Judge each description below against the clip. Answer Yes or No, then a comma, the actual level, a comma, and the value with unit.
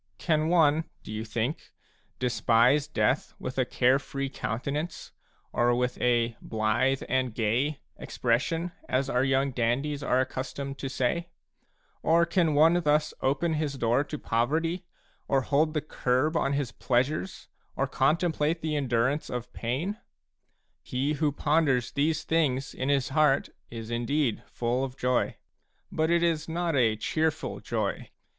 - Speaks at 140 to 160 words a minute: Yes, average, 150 wpm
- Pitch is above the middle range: No, medium, 140 Hz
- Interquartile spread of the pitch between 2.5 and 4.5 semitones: Yes, average, 3.8 semitones